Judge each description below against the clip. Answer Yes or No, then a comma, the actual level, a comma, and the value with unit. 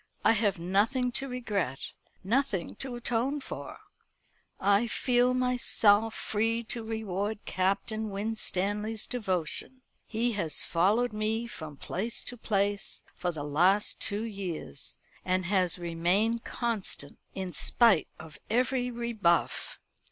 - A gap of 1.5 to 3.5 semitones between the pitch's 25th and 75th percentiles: No, average, 4.0 semitones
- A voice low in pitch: No, high, 210 Hz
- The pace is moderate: No, slow, 120 wpm